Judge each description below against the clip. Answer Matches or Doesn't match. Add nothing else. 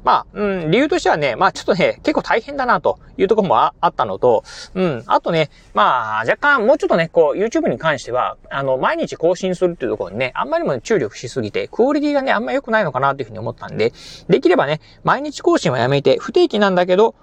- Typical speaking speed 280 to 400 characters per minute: Doesn't match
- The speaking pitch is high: Matches